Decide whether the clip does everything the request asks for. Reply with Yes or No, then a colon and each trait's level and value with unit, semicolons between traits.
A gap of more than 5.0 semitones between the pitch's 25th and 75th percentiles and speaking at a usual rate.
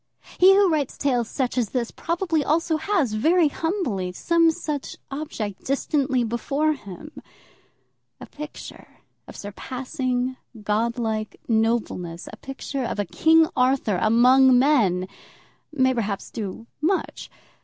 No: wide, 5.6 semitones; slow, 125 wpm